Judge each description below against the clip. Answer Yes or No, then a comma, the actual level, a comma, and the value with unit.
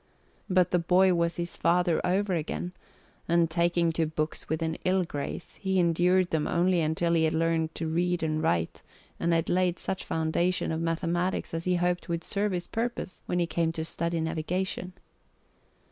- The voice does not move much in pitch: Yes, narrow, 1.8 semitones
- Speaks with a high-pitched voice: No, medium, 170 Hz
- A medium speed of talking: Yes, average, 180 wpm